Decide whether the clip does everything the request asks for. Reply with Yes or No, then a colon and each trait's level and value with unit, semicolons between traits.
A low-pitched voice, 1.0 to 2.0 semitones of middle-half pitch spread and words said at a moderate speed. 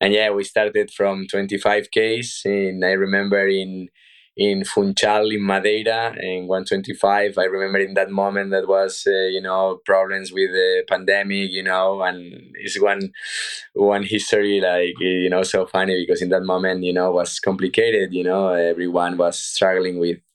Yes: very low, 95 Hz; narrow, 1.7 semitones; average, 170 wpm